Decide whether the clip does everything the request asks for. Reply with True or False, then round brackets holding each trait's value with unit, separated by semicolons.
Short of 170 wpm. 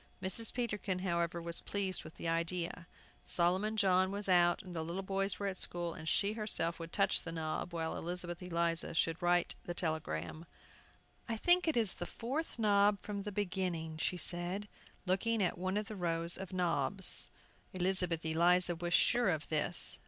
False (175 wpm)